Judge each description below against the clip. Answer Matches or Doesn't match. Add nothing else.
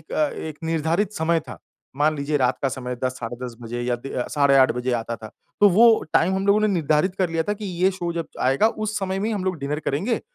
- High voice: Doesn't match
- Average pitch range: Doesn't match